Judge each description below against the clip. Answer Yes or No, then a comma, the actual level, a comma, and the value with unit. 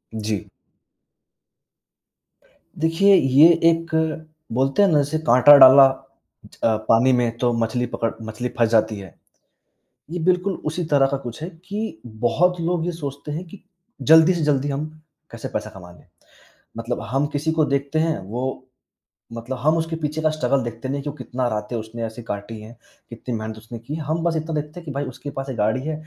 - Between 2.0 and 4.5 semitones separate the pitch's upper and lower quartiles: No, average, 5.3 semitones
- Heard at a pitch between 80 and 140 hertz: Yes, low, 135 Hz